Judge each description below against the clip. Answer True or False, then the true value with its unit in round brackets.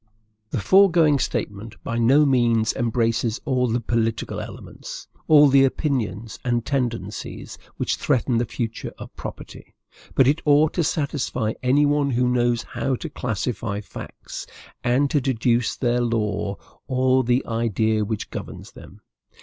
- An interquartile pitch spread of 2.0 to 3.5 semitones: True (3.2 semitones)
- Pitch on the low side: True (120 Hz)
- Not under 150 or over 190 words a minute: False (140 wpm)